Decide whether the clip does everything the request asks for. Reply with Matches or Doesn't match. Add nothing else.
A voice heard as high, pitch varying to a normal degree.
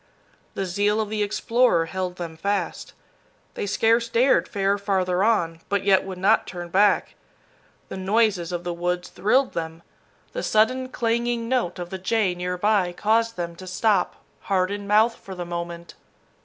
Matches